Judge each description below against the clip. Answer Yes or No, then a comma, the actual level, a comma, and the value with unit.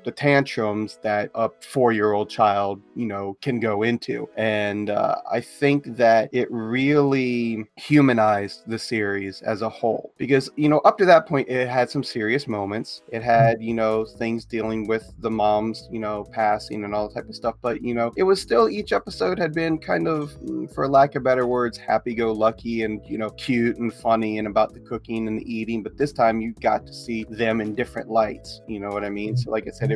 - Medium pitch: No, low, 115 Hz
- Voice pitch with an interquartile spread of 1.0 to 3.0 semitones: Yes, average, 2.7 semitones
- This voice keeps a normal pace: No, fast, 210 wpm